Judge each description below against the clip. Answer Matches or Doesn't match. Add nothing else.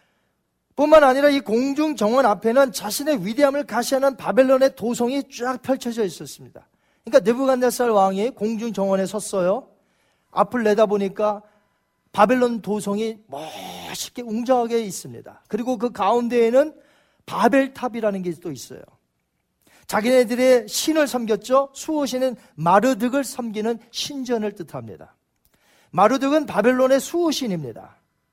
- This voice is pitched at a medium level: Doesn't match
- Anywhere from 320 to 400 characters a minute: Doesn't match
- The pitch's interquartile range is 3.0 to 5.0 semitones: Matches